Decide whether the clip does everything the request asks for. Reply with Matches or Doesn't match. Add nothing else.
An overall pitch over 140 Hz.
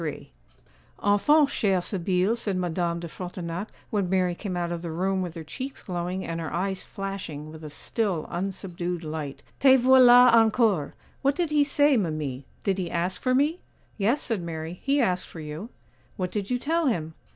Matches